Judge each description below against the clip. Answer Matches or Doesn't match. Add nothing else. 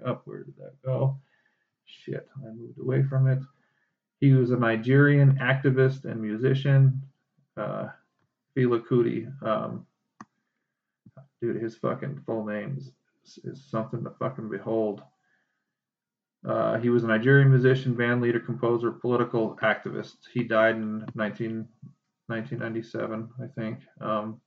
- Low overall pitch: Matches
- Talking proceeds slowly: Matches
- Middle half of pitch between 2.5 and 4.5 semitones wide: Matches